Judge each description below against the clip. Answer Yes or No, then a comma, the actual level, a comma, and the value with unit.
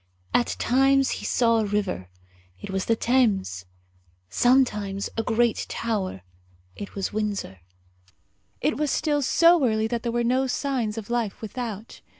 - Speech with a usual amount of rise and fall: Yes, average, 3.7 semitones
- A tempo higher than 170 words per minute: No, average, 150 wpm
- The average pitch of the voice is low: No, high, 230 Hz